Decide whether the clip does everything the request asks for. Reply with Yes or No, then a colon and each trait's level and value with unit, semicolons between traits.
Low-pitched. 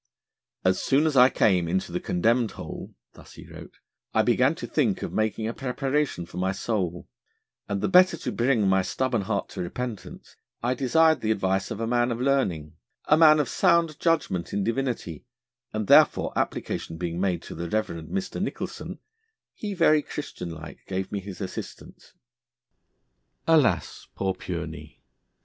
Yes: low, 110 Hz